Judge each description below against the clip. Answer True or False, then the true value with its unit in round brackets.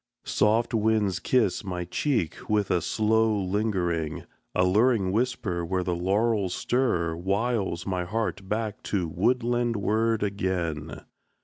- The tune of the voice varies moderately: True (3.8 semitones)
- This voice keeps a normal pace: False (125 wpm)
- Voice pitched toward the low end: True (100 Hz)